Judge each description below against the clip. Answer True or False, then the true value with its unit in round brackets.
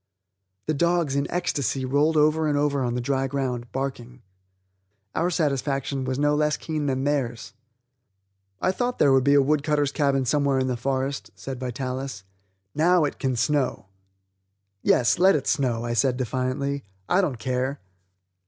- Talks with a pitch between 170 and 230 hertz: False (140 Hz)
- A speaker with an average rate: True (160 wpm)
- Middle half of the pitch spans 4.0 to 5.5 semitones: False (2.4 semitones)